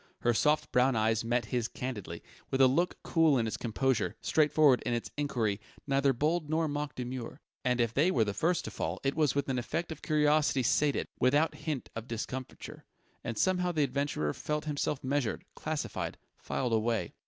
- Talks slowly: No, average, 185 wpm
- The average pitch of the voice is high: No, low, 135 Hz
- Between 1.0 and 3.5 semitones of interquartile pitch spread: No, average, 4.0 semitones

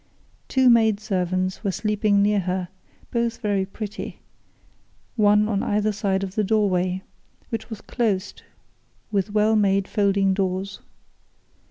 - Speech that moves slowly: Yes, slow, 130 wpm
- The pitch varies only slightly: Yes, narrow, 1.9 semitones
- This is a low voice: No, high, 205 Hz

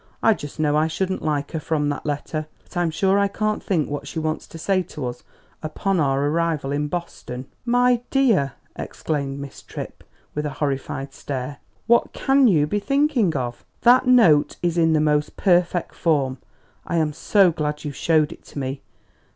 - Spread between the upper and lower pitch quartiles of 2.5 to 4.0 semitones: No, average, 4.6 semitones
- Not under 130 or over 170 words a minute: No, average, 185 wpm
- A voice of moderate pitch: Yes, medium, 155 Hz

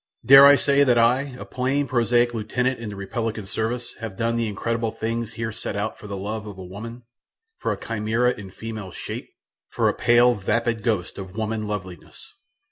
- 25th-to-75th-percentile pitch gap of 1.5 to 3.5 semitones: Yes, narrow, 2.4 semitones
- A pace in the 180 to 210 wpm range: Yes, average, 195 wpm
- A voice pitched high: No, low, 115 Hz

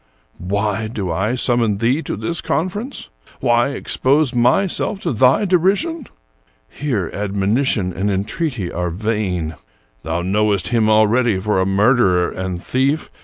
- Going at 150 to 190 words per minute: No, average, 140 wpm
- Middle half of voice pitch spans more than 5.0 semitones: Yes, wide, 5.5 semitones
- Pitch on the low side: Yes, low, 110 Hz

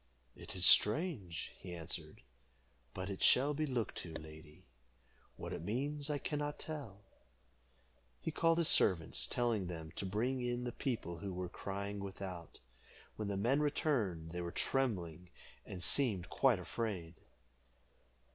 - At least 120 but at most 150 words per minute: Yes, average, 145 wpm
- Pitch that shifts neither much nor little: No, wide, 7.1 semitones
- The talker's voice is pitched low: Yes, low, 100 Hz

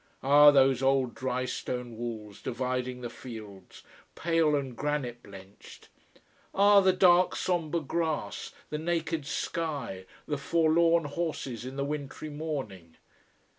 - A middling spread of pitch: Yes, average, 4.7 semitones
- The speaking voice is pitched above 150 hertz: No, medium, 140 Hz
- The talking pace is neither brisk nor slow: No, slow, 120 wpm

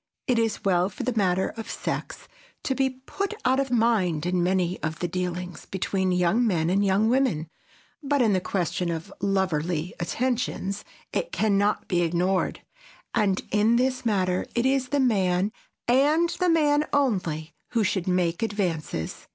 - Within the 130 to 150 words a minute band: No, average, 165 wpm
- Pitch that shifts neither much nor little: No, wide, 5.7 semitones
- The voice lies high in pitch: Yes, high, 195 Hz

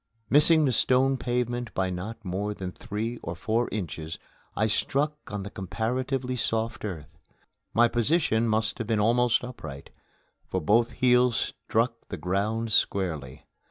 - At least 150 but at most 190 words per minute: No, average, 140 wpm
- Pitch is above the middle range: No, low, 115 Hz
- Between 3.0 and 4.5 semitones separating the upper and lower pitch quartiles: Yes, average, 3.9 semitones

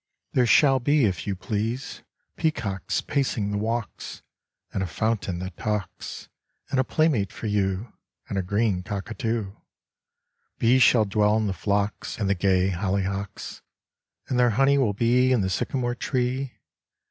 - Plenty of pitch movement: No, average, 4.1 semitones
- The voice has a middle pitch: No, low, 105 Hz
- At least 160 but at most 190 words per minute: No, average, 150 wpm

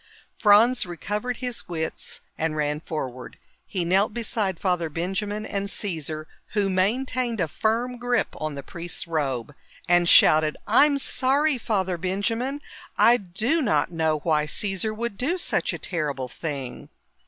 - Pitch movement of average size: No, wide, 6.4 semitones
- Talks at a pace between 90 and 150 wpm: Yes, average, 140 wpm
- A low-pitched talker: No, high, 190 Hz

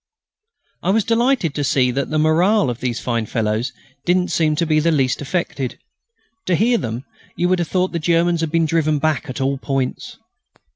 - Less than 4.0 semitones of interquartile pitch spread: No, average, 4.7 semitones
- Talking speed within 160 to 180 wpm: No, average, 190 wpm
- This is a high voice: No, medium, 155 Hz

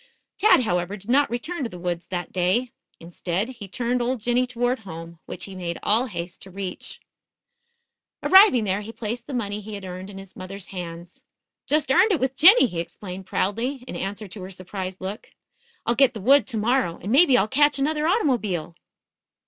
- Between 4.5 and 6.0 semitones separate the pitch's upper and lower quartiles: Yes, wide, 5.5 semitones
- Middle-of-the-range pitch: No, high, 210 Hz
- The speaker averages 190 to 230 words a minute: Yes, average, 195 wpm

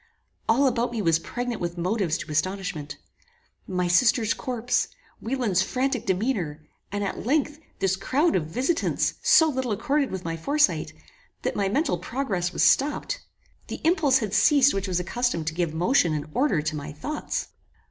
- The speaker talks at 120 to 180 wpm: Yes, average, 165 wpm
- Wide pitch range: Yes, wide, 7.2 semitones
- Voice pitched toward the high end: Yes, high, 210 Hz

